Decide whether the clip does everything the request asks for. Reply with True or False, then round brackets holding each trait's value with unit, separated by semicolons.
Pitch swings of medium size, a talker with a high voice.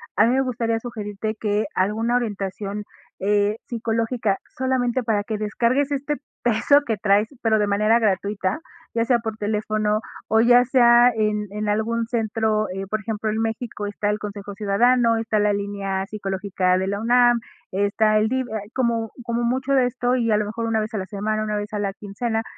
False (2.2 semitones; 215 Hz)